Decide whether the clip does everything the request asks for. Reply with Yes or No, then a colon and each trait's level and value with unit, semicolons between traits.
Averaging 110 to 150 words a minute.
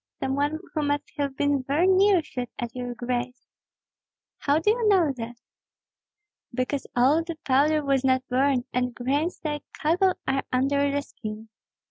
No: average, 160 wpm